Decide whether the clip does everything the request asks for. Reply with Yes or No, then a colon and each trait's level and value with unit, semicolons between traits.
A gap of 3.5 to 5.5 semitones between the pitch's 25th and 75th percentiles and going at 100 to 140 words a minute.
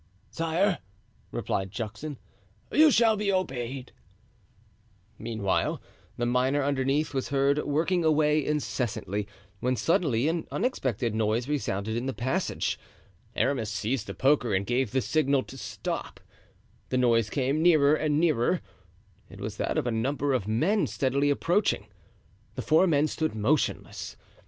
Yes: average, 4.7 semitones; slow, 135 wpm